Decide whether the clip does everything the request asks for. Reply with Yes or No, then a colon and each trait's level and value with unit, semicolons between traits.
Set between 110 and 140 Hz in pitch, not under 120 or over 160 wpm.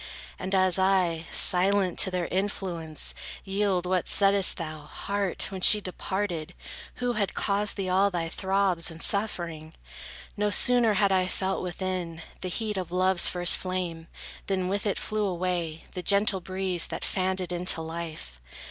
No: medium, 185 Hz; average, 155 wpm